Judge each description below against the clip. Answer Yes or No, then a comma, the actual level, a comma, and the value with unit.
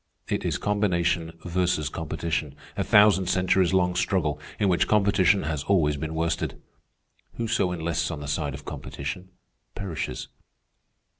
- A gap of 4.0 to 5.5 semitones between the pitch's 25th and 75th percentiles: No, average, 3.3 semitones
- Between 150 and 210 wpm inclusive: No, slow, 135 wpm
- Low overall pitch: Yes, very low, 85 Hz